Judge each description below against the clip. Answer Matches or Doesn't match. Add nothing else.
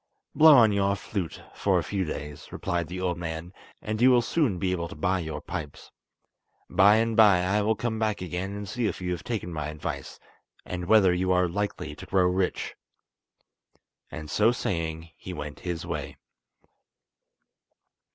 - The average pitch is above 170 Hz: Doesn't match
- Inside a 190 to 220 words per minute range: Doesn't match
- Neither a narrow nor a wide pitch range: Matches